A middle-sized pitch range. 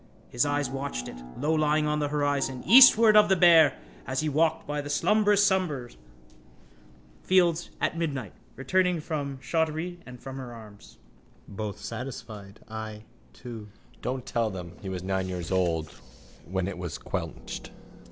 No: wide, 6.9 semitones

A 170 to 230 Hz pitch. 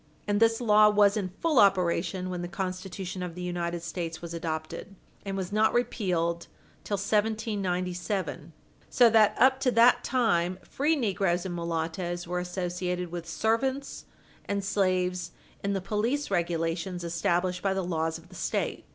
Yes: medium, 185 Hz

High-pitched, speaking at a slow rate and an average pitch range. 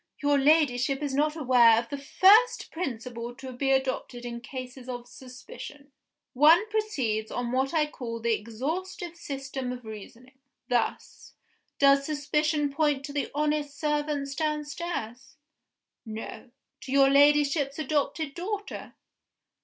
Yes: very high, 275 Hz; slow, 130 wpm; average, 3.3 semitones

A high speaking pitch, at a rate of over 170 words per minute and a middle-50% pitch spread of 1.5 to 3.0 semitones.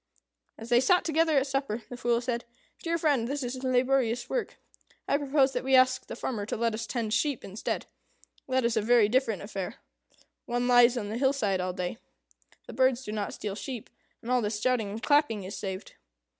No: high, 245 Hz; average, 200 wpm; average, 3.4 semitones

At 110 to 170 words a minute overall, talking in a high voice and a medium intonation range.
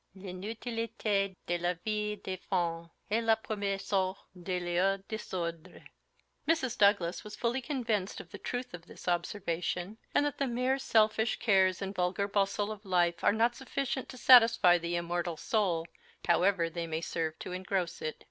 Yes: average, 165 wpm; high, 195 Hz; average, 4.1 semitones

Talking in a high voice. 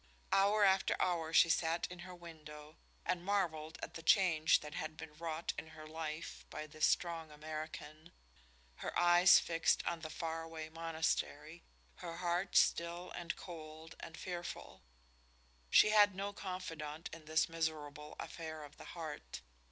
No: medium, 165 Hz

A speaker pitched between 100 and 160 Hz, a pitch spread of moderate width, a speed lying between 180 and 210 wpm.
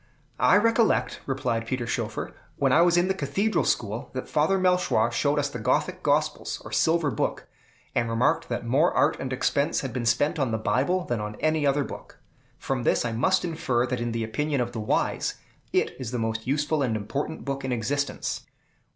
Yes: low, 135 Hz; average, 4.5 semitones; average, 200 wpm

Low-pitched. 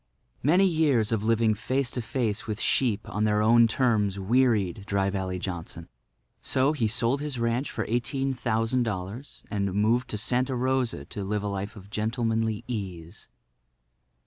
Yes: low, 110 Hz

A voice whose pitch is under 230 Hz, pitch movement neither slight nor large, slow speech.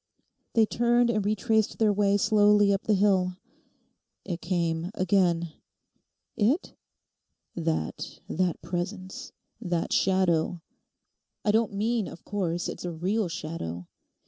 Yes: high, 190 Hz; average, 3.6 semitones; slow, 115 wpm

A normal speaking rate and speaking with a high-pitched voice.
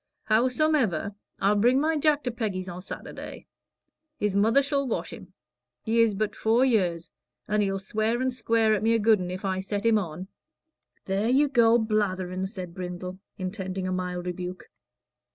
Yes: average, 175 wpm; high, 210 Hz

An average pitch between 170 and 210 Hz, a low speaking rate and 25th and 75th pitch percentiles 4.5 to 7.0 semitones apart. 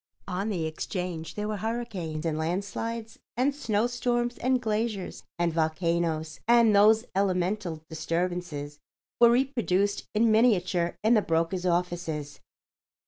Yes: high, 190 Hz; slow, 120 wpm; average, 5.1 semitones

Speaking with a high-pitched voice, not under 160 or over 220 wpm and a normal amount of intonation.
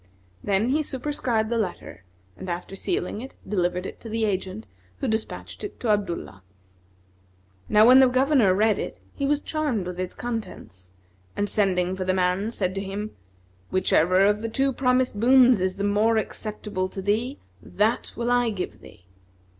Yes: high, 210 Hz; average, 170 wpm; average, 4.5 semitones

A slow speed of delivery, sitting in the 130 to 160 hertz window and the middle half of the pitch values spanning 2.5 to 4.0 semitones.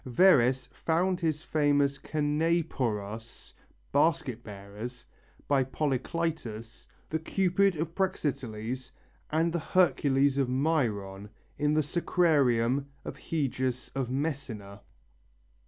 No: slow, 95 wpm; medium, 140 Hz; average, 5.0 semitones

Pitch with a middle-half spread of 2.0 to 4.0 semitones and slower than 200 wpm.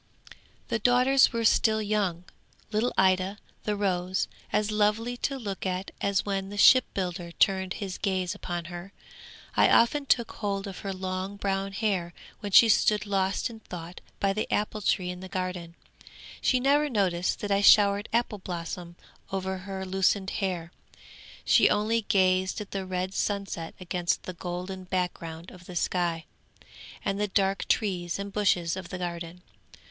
Yes: narrow, 2.4 semitones; average, 160 wpm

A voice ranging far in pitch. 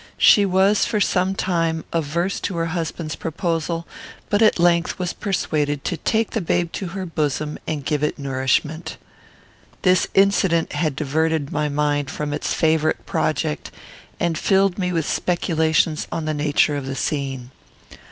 No: average, 3.3 semitones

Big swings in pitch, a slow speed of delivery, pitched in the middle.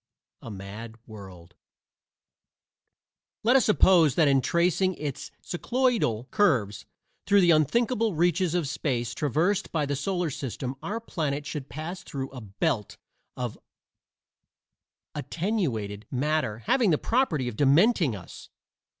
Yes: wide, 7.1 semitones; slow, 125 wpm; medium, 150 Hz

